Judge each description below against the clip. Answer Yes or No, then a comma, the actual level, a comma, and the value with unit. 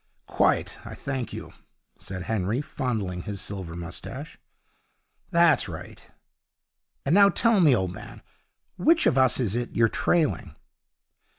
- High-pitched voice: No, low, 120 Hz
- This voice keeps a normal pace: No, slow, 130 wpm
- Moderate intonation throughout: No, wide, 8.2 semitones